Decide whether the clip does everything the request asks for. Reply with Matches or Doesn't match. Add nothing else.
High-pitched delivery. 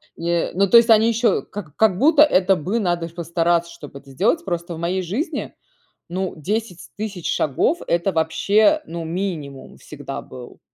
Doesn't match